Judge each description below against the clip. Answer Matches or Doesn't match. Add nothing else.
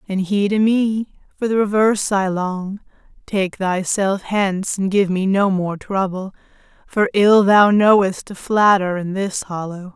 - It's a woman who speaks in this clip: Matches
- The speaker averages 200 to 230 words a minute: Doesn't match